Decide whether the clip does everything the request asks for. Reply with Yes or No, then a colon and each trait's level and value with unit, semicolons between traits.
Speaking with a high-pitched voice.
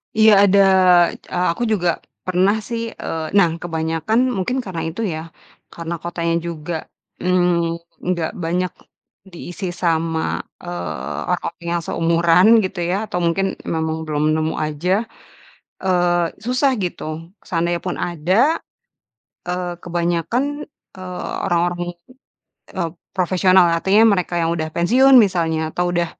No: medium, 175 Hz